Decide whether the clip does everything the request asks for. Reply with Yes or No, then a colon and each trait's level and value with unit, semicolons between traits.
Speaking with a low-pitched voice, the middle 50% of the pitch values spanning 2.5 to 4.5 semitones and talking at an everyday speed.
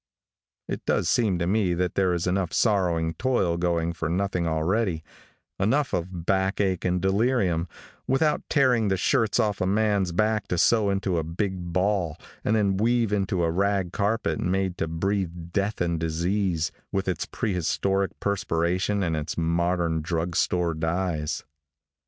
Yes: very low, 90 Hz; average, 3.1 semitones; average, 160 wpm